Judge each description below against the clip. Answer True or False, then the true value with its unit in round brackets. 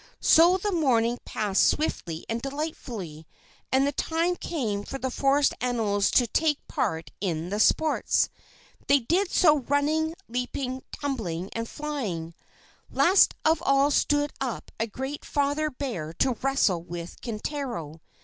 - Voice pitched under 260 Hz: False (265 Hz)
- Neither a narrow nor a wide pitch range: False (6.2 semitones)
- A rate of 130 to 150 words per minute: True (140 wpm)